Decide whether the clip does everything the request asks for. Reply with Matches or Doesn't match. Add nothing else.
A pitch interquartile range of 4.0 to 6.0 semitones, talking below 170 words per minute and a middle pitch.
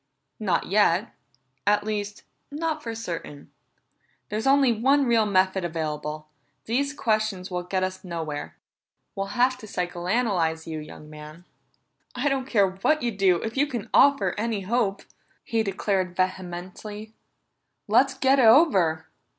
Doesn't match